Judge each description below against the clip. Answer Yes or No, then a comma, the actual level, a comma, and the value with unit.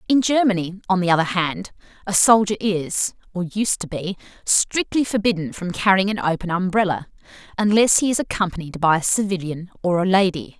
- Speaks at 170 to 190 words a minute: No, average, 160 wpm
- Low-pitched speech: No, high, 190 Hz